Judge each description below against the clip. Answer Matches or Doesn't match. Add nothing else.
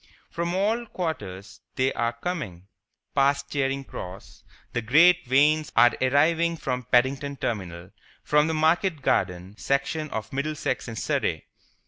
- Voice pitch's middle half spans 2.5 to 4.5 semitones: Doesn't match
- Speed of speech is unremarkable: Doesn't match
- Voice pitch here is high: Doesn't match